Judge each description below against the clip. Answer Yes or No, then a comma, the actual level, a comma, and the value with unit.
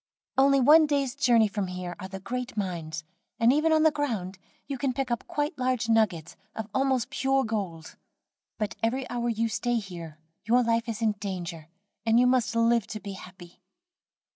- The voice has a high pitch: Yes, high, 230 Hz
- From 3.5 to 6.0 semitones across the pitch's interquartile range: Yes, average, 5.1 semitones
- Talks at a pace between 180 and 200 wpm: Yes, average, 185 wpm